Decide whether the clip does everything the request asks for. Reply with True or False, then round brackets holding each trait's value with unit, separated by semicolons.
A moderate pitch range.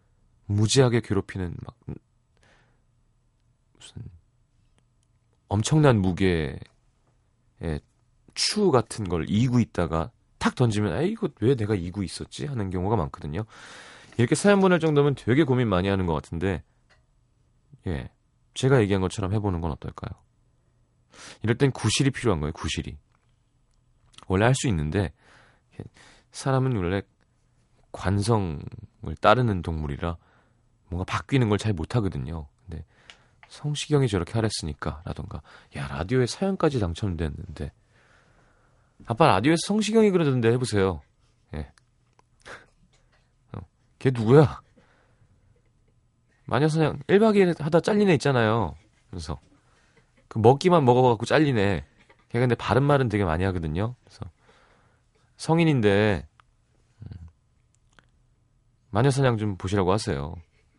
True (4.9 semitones)